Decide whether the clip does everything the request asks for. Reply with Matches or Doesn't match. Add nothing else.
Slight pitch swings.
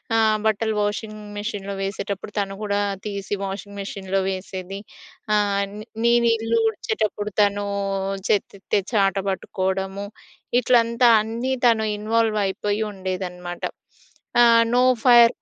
Matches